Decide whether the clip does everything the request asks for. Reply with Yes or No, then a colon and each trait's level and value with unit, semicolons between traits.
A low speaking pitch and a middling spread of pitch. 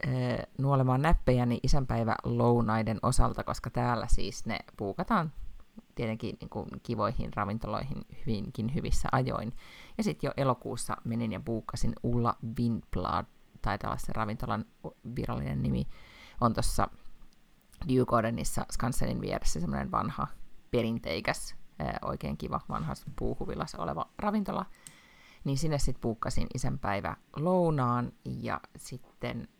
Yes: low, 120 Hz; average, 3.4 semitones